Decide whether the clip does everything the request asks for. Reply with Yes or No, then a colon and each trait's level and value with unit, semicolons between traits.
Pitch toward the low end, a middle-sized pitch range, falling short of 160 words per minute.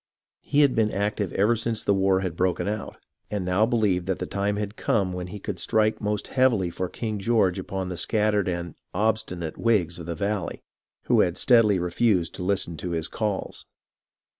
No: low, 100 Hz; average, 3.0 semitones; average, 190 wpm